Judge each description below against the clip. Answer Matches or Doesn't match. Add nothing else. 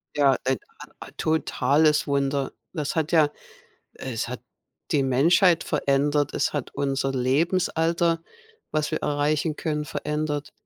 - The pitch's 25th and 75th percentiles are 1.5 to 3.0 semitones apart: Matches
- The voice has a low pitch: Doesn't match